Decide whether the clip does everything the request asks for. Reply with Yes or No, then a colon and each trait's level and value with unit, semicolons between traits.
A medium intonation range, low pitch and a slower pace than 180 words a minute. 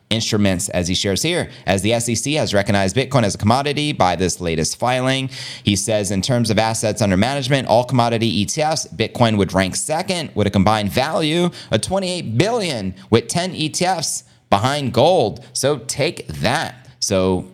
No: wide, 6.3 semitones; low, 115 Hz; average, 170 wpm